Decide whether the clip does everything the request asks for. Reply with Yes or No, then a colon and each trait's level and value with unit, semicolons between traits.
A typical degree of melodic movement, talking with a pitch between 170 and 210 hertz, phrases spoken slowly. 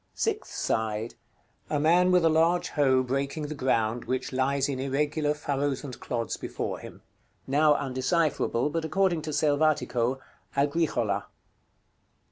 No: average, 3.3 semitones; medium, 145 Hz; slow, 130 wpm